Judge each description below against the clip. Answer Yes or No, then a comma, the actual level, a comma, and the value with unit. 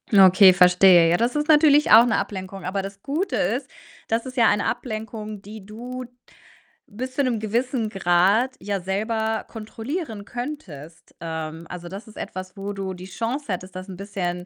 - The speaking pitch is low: No, high, 205 Hz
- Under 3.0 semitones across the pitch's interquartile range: No, average, 4.1 semitones